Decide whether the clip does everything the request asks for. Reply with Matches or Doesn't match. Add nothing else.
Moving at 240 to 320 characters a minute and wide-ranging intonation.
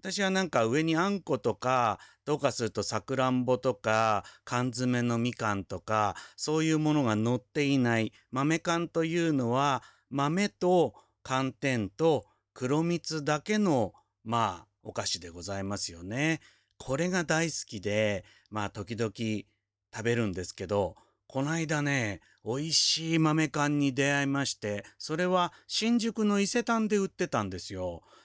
Matches